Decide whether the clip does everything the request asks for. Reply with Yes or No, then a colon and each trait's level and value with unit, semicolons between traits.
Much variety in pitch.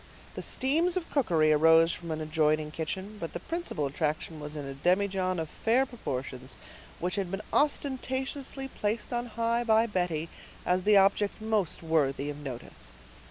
Yes: wide, 6.9 semitones